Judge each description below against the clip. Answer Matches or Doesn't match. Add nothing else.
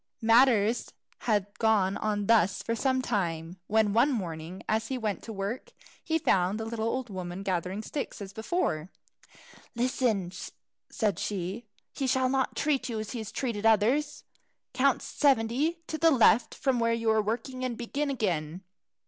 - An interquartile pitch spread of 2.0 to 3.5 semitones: Doesn't match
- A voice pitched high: Matches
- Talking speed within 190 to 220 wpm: Doesn't match